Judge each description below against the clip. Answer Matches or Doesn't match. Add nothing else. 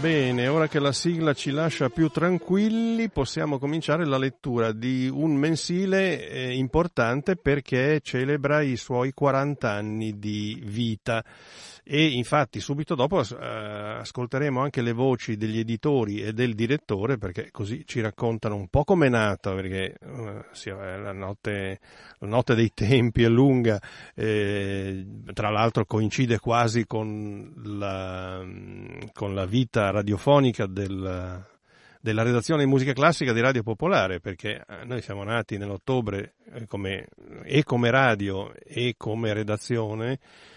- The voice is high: Doesn't match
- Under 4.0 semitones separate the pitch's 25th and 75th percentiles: Doesn't match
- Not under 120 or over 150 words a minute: Matches